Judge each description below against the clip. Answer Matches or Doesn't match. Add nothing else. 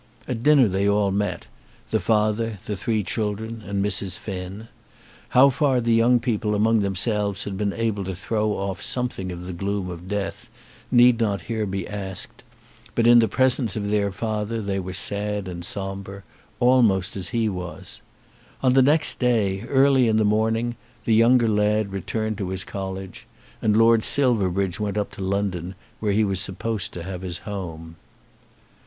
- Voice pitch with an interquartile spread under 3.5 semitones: Matches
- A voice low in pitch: Matches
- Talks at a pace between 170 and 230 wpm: Matches